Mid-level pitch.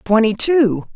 No: high, 225 Hz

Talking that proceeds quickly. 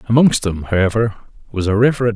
No: average, 165 wpm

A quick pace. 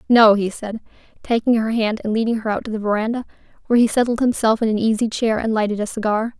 Yes: fast, 235 wpm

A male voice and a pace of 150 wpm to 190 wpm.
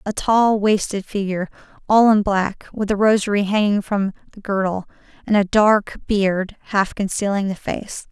No: female; average, 165 wpm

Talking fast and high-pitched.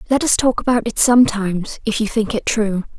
Yes: fast, 220 wpm; high, 225 Hz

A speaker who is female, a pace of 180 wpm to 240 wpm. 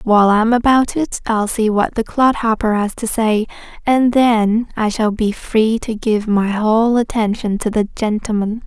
Yes: female; average, 185 wpm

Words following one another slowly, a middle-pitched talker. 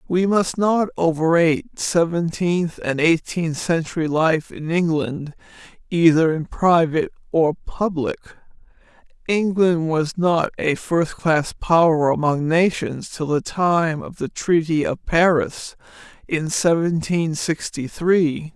Yes: slow, 115 wpm; medium, 165 Hz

